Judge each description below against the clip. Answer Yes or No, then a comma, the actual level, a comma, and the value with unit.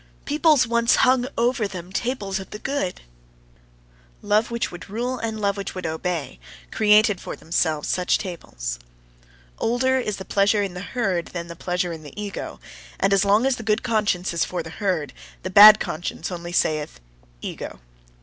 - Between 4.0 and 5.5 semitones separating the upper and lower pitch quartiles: Yes, average, 4.5 semitones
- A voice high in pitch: Yes, high, 200 Hz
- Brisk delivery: No, average, 175 wpm